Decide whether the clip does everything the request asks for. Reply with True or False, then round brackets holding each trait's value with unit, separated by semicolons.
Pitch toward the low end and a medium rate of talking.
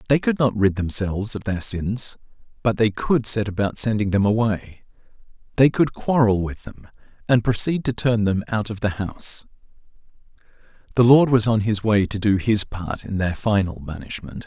True (105 Hz; 185 wpm)